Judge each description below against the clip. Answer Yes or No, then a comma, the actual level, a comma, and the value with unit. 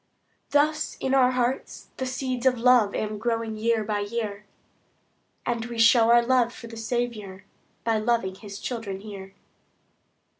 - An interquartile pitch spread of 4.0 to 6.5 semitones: No, average, 2.8 semitones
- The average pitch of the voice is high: Yes, high, 230 Hz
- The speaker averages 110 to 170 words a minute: Yes, average, 150 wpm